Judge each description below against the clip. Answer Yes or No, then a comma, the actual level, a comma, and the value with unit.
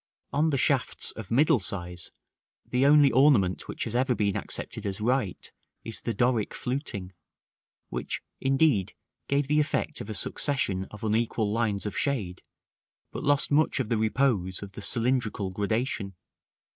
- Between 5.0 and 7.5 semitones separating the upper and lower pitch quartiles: Yes, average, 5.3 semitones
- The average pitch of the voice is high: No, low, 115 Hz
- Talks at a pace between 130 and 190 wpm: Yes, average, 160 wpm